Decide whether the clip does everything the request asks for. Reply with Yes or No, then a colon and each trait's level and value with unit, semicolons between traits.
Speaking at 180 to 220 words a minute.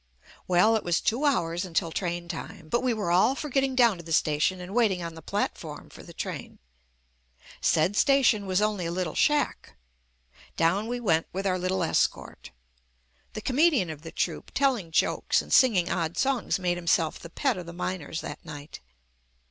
Yes: average, 190 wpm